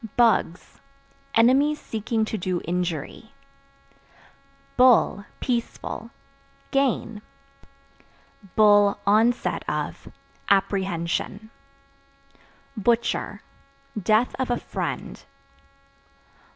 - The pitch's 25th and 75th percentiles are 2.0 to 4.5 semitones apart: Yes, average, 3.3 semitones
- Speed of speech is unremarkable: No, slow, 60 wpm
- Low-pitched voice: No, high, 220 Hz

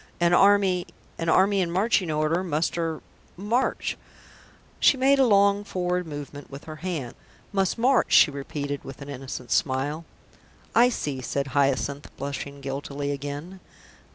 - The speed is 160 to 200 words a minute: No, average, 145 wpm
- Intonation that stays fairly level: No, average, 5.2 semitones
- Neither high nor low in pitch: Yes, medium, 160 Hz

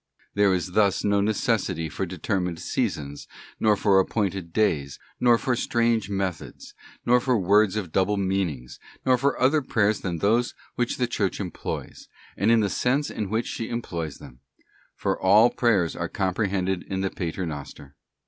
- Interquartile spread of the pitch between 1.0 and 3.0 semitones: No, average, 3.9 semitones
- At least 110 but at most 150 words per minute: No, average, 165 wpm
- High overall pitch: No, low, 100 Hz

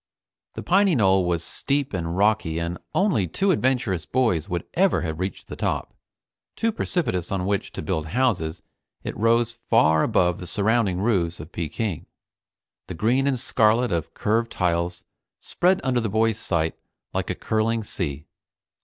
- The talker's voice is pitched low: Yes, low, 100 Hz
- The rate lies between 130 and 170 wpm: Yes, average, 160 wpm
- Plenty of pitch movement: Yes, wide, 5.8 semitones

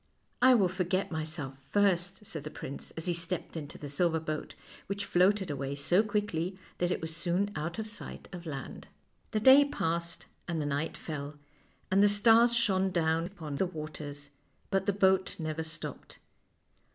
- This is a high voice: No, medium, 175 Hz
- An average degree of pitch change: Yes, average, 4.0 semitones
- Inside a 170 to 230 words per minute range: Yes, average, 175 wpm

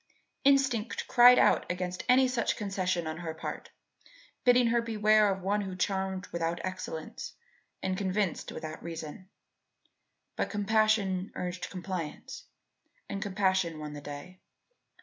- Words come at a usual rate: No, slow, 130 wpm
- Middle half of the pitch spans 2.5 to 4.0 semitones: Yes, average, 3.3 semitones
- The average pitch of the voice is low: No, high, 190 Hz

